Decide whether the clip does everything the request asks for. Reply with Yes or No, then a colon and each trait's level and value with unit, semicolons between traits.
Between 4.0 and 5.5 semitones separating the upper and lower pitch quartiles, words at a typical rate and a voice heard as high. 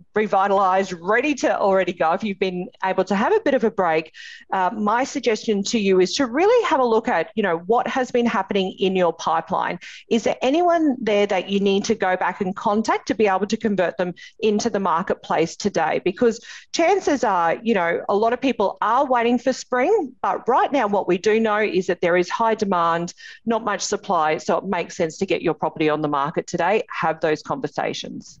No: average, 4.6 semitones; fast, 220 wpm; high, 205 Hz